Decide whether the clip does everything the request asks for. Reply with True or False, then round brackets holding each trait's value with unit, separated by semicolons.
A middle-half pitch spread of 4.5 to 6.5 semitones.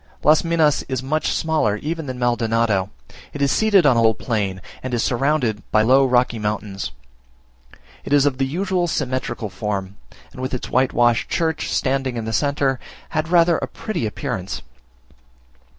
True (5.1 semitones)